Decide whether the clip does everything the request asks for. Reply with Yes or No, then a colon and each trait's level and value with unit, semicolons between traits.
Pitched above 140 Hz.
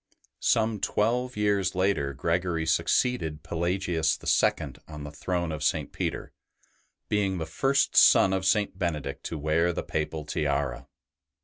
No: very low, 85 Hz